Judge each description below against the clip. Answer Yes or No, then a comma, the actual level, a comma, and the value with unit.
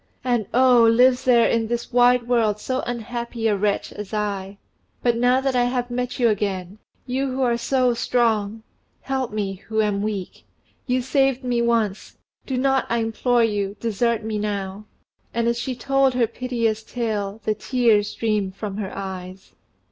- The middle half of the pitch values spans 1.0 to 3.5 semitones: Yes, average, 3.0 semitones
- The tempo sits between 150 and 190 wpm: Yes, average, 170 wpm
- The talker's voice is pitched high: Yes, high, 230 Hz